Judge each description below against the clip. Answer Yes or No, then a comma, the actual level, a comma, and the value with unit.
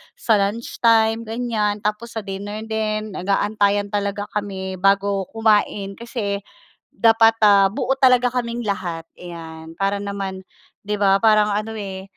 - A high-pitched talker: Yes, high, 205 Hz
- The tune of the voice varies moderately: No, narrow, 2.1 semitones